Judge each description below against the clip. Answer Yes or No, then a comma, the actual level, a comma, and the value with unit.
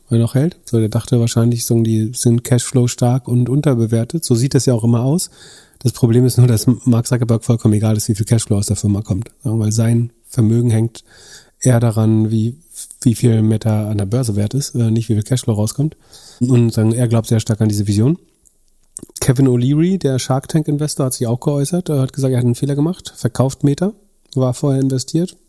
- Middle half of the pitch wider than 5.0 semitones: No, average, 3.0 semitones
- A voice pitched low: Yes, low, 120 Hz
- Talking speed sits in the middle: No, fast, 210 wpm